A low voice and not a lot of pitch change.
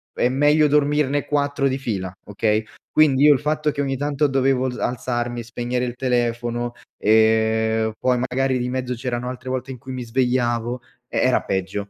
Yes: low, 125 Hz; narrow, 2.3 semitones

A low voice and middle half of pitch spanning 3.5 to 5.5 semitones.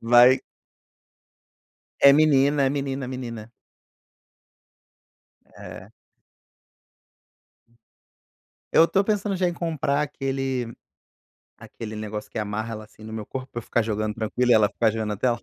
Yes: low, 125 Hz; average, 4.2 semitones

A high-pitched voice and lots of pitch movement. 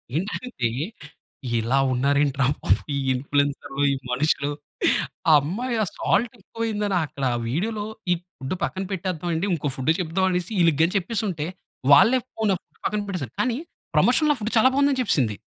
No: medium, 180 Hz; wide, 7.2 semitones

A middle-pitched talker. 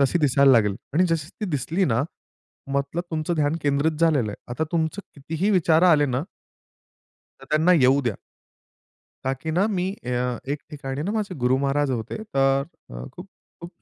Yes: medium, 145 Hz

